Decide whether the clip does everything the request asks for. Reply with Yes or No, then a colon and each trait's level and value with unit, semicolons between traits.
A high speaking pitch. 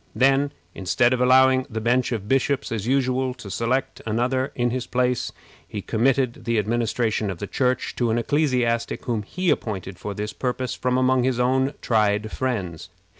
No: low, 125 Hz